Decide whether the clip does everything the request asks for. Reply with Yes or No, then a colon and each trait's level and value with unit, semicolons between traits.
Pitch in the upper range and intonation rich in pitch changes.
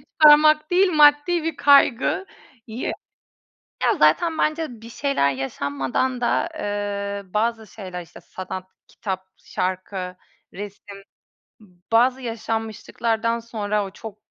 Yes: high, 225 Hz; wide, 6.1 semitones